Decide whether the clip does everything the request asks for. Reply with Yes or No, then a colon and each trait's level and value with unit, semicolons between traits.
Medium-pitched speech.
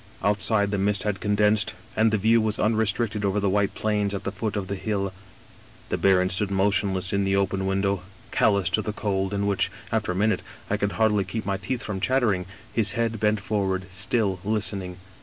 No: low, 100 Hz